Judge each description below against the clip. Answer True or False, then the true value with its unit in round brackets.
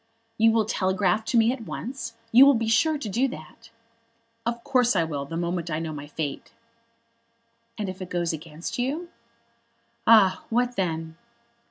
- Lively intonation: True (6.1 semitones)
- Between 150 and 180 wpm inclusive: True (170 wpm)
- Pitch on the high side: True (210 Hz)